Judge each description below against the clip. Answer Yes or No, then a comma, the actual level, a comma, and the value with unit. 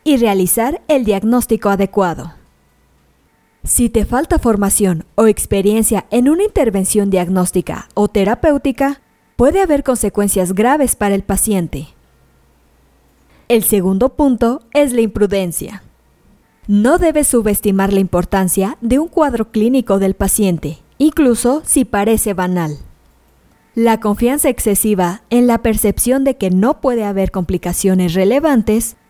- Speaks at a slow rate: Yes, slow, 120 wpm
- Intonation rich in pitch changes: No, average, 4.6 semitones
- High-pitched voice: Yes, high, 210 Hz